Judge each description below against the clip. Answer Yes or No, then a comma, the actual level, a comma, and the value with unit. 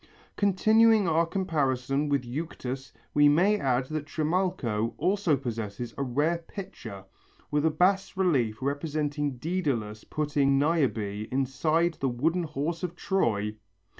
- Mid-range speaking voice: Yes, medium, 145 Hz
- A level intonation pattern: No, average, 5.1 semitones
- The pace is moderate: No, slow, 125 wpm